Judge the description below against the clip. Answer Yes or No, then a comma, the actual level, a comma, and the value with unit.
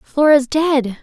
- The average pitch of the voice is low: No, very high, 280 Hz